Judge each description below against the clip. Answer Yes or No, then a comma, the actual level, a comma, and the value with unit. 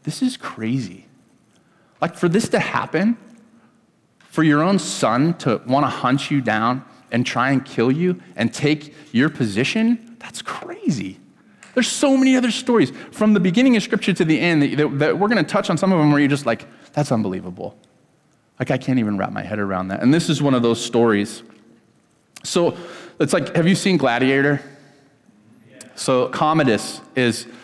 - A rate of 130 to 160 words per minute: No, average, 180 wpm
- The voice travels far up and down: Yes, wide, 8.1 semitones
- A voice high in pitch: No, medium, 145 Hz